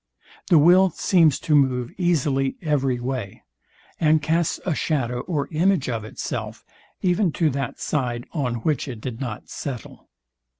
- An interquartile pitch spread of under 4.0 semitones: No, average, 4.7 semitones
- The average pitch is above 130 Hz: Yes, medium, 140 Hz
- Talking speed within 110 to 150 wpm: Yes, average, 145 wpm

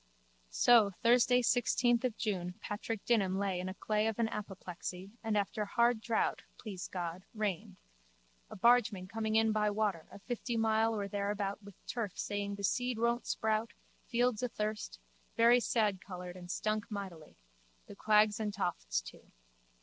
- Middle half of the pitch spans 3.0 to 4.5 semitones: No, narrow, 2.6 semitones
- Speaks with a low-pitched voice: No, high, 210 Hz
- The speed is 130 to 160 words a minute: Yes, average, 150 wpm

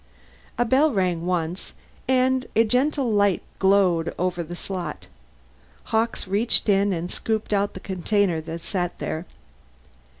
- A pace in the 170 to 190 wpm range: No, average, 140 wpm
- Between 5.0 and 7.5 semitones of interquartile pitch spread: No, average, 4.2 semitones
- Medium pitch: No, high, 195 Hz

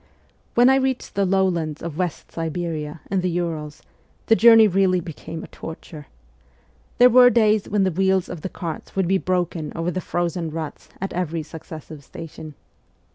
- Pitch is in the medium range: Yes, medium, 175 Hz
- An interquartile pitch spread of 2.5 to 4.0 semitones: Yes, average, 3.1 semitones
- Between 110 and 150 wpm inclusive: No, average, 175 wpm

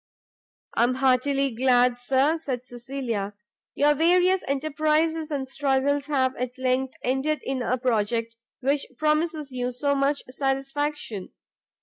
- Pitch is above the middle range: Yes, very high, 270 Hz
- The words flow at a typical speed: No, slow, 125 wpm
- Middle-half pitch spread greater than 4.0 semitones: No, average, 2.7 semitones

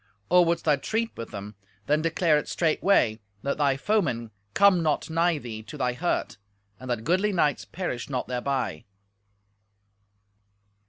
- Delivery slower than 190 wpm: Yes, average, 150 wpm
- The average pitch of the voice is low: No, medium, 150 Hz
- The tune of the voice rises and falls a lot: Yes, wide, 5.9 semitones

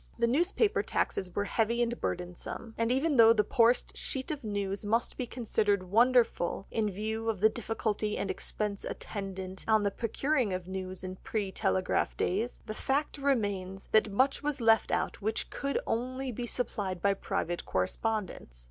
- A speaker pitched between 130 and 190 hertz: No, high, 220 Hz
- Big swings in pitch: No, average, 3.7 semitones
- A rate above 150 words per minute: Yes, average, 165 wpm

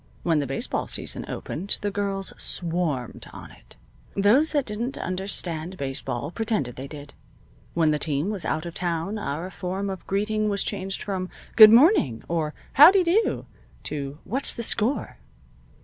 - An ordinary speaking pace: Yes, average, 155 wpm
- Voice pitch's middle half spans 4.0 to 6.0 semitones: Yes, wide, 5.5 semitones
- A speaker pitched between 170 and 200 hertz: Yes, high, 190 Hz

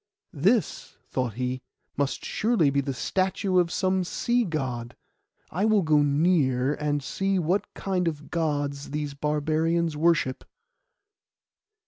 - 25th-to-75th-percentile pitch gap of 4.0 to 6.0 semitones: Yes, average, 4.6 semitones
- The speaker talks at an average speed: No, slow, 125 wpm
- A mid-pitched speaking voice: Yes, medium, 155 Hz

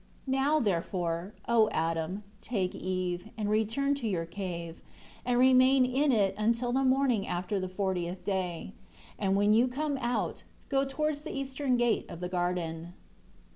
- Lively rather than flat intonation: Yes, wide, 6.2 semitones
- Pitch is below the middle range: No, high, 210 Hz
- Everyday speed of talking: Yes, average, 160 wpm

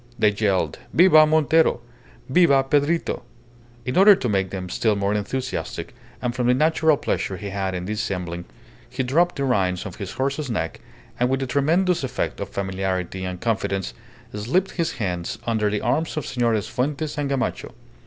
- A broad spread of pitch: Yes, wide, 6.9 semitones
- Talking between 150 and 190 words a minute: Yes, average, 170 wpm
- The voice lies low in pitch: Yes, low, 125 Hz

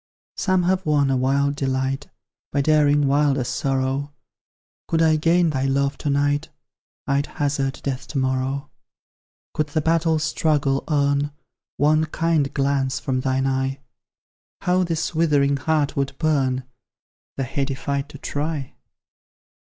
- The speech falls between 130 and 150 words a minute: Yes, slow, 135 wpm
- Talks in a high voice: No, medium, 140 Hz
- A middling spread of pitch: No, narrow, 2.2 semitones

